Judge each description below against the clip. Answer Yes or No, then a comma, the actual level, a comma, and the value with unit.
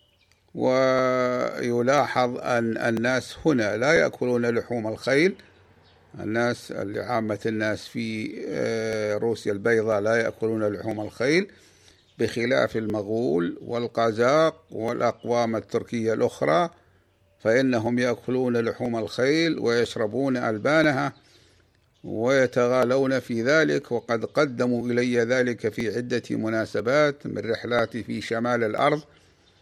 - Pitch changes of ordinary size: No, narrow, 2.1 semitones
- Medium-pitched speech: No, low, 115 Hz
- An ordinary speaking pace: Yes, average, 90 wpm